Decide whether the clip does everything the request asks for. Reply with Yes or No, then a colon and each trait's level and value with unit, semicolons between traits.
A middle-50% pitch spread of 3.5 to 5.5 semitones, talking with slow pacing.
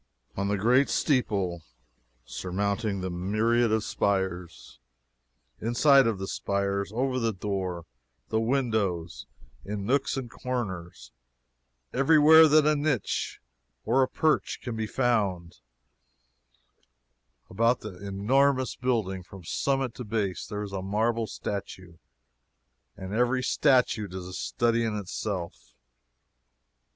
Yes: average, 4.7 semitones; slow, 120 wpm